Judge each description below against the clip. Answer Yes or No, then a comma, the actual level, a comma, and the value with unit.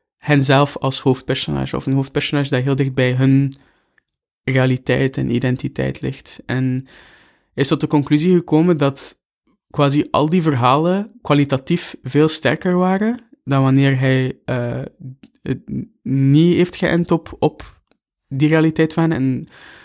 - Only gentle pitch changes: No, average, 3.4 semitones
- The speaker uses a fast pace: No, slow, 130 wpm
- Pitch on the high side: No, medium, 140 Hz